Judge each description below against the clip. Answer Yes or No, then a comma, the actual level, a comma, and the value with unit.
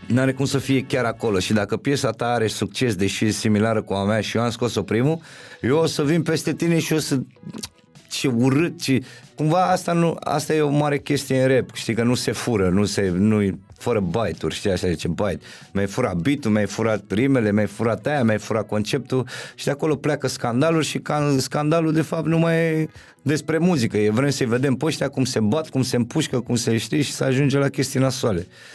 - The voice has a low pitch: Yes, low, 130 Hz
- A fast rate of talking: Yes, fast, 230 wpm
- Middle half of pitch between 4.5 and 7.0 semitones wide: Yes, average, 5.3 semitones